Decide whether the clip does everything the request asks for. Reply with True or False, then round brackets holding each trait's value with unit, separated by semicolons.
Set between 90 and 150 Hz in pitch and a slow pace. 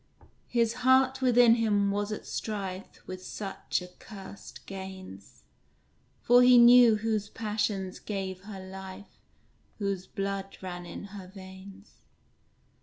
False (200 Hz; 115 wpm)